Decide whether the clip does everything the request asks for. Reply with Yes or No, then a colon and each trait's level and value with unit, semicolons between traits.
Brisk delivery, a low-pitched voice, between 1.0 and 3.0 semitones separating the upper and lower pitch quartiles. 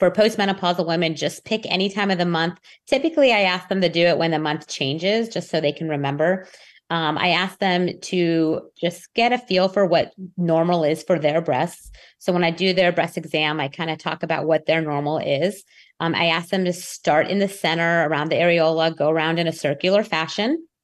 No: fast, 220 wpm; medium, 170 Hz; average, 2.7 semitones